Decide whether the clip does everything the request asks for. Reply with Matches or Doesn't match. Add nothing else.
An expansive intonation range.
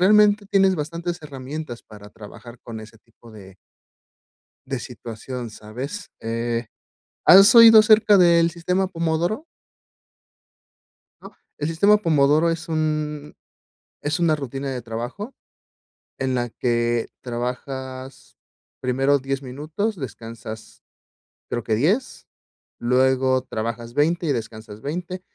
Matches